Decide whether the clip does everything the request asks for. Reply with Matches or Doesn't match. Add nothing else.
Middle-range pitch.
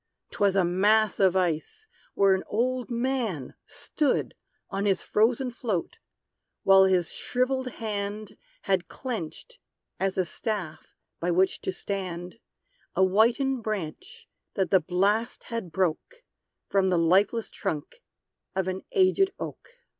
Doesn't match